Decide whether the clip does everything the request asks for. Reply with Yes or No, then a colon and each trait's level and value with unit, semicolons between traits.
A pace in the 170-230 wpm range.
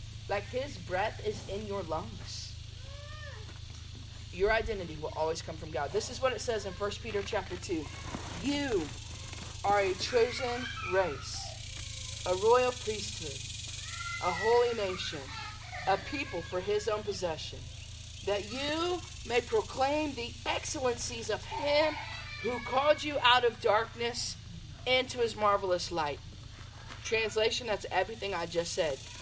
No: slow, 135 wpm